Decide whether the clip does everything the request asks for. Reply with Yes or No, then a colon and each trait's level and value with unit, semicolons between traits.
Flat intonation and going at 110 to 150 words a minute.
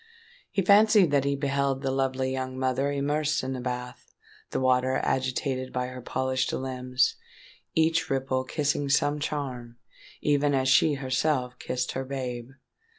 Yes: narrow, 1.7 semitones; average, 140 wpm